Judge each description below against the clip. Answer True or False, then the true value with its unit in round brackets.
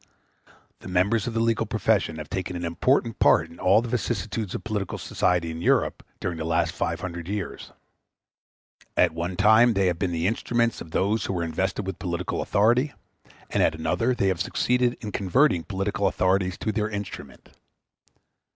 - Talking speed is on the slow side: False (180 wpm)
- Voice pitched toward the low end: True (95 Hz)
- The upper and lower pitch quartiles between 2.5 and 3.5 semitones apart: False (4.4 semitones)